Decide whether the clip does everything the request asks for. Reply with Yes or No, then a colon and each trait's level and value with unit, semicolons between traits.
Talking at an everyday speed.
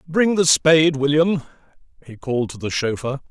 Yes: average, 165 wpm